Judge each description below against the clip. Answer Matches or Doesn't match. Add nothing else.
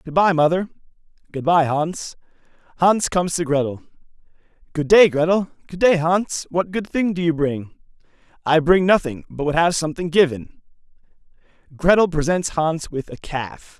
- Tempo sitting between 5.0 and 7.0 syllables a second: Doesn't match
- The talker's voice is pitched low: Doesn't match